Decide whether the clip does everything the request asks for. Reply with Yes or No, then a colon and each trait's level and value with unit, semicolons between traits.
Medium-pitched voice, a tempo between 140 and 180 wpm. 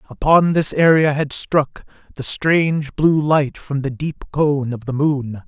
Yes: medium, 145 Hz; average, 175 wpm